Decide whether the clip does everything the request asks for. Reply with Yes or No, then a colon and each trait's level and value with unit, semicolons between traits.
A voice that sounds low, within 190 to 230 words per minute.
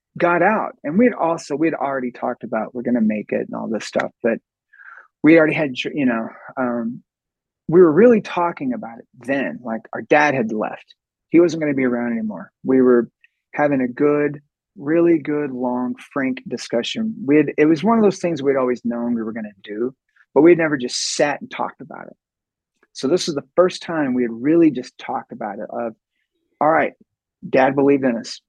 No: medium, 145 Hz; average, 200 wpm